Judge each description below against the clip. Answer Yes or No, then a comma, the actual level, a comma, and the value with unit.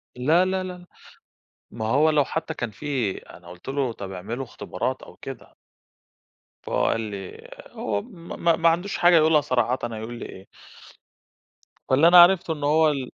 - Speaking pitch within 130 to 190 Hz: Yes, medium, 140 Hz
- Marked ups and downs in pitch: Yes, wide, 6.4 semitones